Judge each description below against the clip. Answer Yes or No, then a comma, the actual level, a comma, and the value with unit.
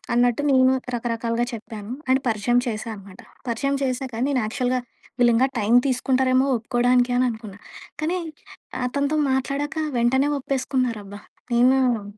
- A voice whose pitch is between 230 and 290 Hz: Yes, high, 245 Hz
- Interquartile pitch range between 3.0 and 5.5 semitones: No, narrow, 2.4 semitones